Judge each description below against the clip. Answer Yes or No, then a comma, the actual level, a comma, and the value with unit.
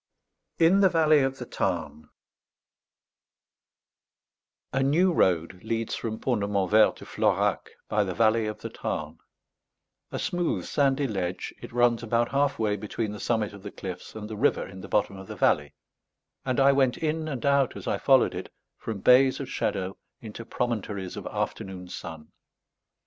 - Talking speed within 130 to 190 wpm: Yes, average, 170 wpm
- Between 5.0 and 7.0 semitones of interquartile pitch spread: Yes, wide, 5.5 semitones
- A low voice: Yes, low, 115 Hz